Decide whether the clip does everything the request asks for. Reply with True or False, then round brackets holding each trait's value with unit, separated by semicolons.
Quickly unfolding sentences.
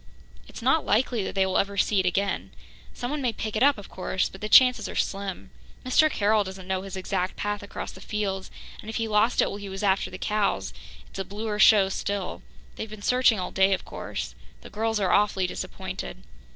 True (220 wpm)